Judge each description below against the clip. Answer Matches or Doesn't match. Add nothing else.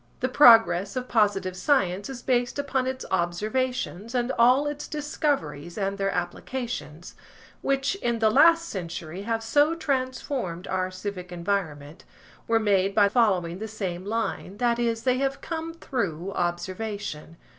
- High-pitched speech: Matches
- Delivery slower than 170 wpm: Matches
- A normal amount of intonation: Doesn't match